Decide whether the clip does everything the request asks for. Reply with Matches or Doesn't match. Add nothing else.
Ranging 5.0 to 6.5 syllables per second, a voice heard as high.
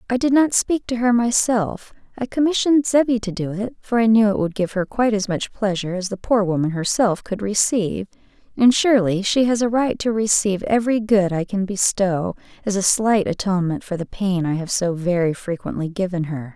Matches